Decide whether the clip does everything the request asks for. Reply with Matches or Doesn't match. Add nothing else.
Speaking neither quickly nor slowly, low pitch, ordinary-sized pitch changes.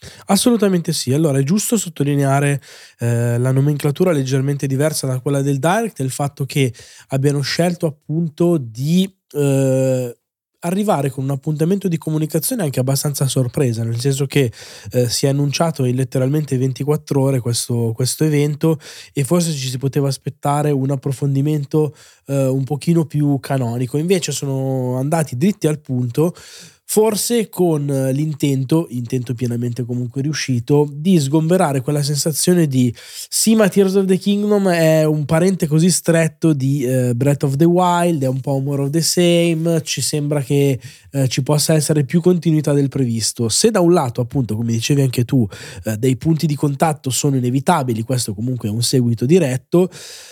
Doesn't match